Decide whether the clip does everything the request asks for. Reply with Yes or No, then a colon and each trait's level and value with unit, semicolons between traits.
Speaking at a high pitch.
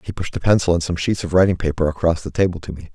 No: very low, 85 Hz